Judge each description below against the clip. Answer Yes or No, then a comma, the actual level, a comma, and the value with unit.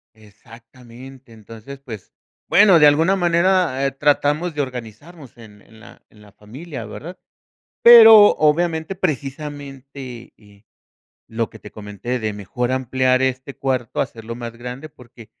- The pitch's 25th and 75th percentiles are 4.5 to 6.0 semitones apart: Yes, average, 4.8 semitones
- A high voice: No, low, 130 Hz